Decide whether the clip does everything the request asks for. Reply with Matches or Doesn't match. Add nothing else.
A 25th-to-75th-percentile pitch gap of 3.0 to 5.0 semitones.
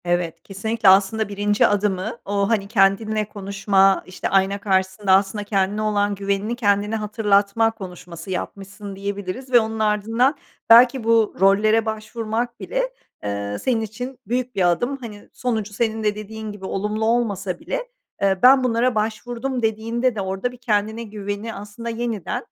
Doesn't match